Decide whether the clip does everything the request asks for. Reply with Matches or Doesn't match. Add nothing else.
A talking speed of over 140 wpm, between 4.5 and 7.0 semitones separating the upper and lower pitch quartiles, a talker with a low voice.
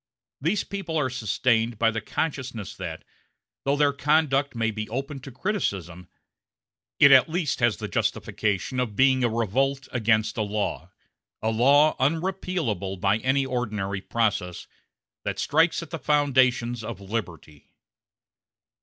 Doesn't match